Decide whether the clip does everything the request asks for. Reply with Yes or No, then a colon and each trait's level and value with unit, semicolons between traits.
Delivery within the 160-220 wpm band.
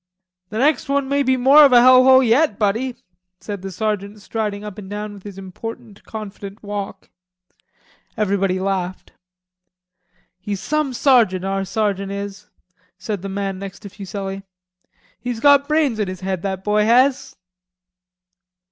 No: average, 150 wpm